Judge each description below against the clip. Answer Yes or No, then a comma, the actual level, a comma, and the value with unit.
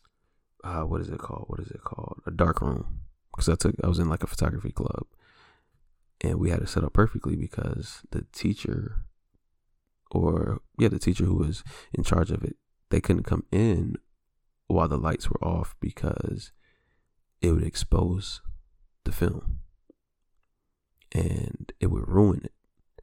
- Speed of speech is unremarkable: Yes, average, 160 wpm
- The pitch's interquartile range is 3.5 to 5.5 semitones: Yes, average, 3.9 semitones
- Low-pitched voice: Yes, very low, 85 Hz